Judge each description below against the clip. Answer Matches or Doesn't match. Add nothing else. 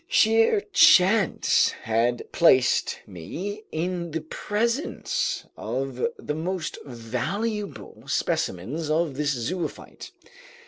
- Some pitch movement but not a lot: Doesn't match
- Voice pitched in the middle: Matches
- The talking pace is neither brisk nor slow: Doesn't match